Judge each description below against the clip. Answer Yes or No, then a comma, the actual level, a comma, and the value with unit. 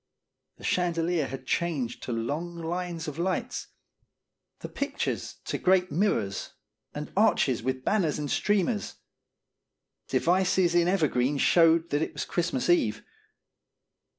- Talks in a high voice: No, medium, 170 Hz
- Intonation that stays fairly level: No, average, 4.1 semitones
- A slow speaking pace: Yes, slow, 125 wpm